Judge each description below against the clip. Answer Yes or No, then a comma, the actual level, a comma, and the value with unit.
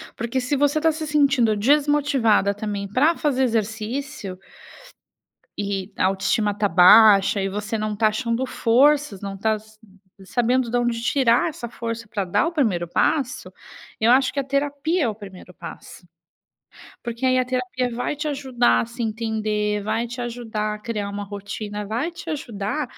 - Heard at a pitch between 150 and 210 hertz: No, high, 230 Hz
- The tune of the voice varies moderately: Yes, average, 4.3 semitones